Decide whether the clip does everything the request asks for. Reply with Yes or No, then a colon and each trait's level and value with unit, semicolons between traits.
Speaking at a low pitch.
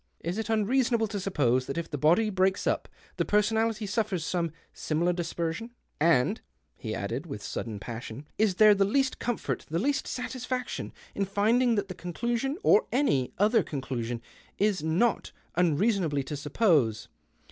No: high, 190 Hz